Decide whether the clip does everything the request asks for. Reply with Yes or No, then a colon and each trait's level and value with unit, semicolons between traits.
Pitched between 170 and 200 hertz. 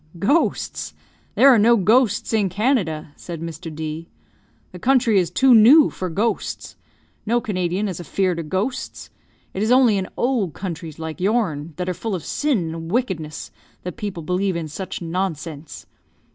Yes: medium, 185 Hz